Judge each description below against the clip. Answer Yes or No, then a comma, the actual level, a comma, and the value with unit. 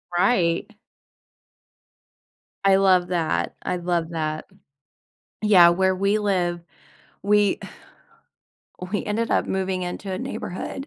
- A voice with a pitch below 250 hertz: Yes, medium, 185 Hz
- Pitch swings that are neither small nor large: No, narrow, 2.3 semitones